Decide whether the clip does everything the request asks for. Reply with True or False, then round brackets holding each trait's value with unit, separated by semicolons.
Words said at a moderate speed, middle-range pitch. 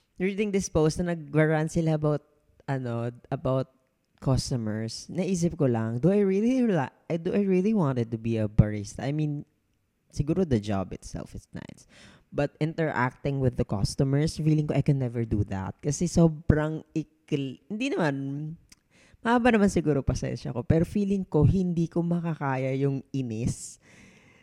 True (155 wpm; 150 Hz)